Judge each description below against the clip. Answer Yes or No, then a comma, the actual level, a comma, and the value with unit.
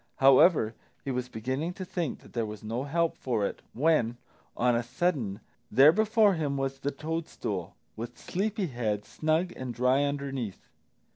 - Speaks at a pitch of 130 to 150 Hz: Yes, low, 135 Hz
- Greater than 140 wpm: Yes, average, 160 wpm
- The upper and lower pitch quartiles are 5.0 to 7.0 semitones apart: Yes, average, 5.3 semitones